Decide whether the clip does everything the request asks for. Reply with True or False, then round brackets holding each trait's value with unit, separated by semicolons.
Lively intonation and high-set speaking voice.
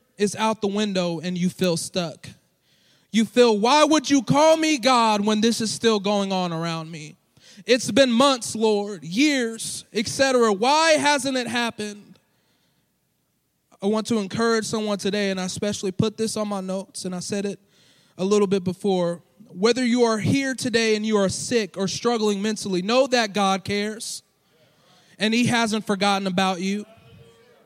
False (3.5 semitones; 210 Hz)